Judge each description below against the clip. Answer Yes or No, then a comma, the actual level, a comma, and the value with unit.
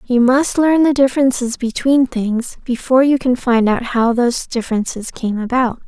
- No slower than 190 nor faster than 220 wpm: No, average, 175 wpm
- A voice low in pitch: No, high, 245 Hz